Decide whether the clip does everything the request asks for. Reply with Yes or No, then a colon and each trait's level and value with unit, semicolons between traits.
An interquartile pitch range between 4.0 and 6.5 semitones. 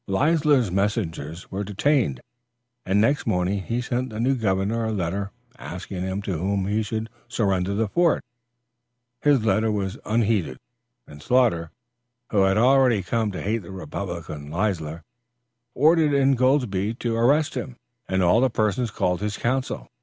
Yes: average, 4.4 semitones